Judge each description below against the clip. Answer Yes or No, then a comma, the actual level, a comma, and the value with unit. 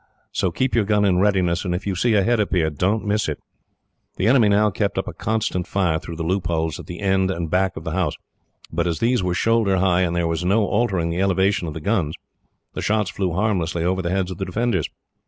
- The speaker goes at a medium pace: No, fast, 240 wpm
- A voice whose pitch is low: Yes, very low, 95 Hz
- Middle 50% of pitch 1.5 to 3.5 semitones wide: Yes, average, 3.1 semitones